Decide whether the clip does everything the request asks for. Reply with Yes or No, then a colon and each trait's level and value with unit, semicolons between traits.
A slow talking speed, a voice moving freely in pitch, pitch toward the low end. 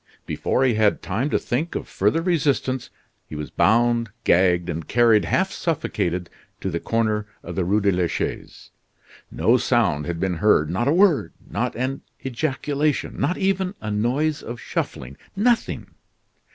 No: average, 160 wpm; wide, 7.4 semitones; low, 115 Hz